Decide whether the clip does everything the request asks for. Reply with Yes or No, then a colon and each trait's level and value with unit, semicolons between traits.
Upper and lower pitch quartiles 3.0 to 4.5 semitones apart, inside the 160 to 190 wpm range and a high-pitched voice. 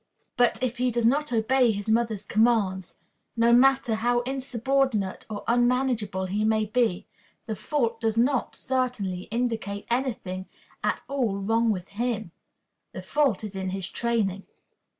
No: average, 3.5 semitones; average, 150 wpm; high, 230 Hz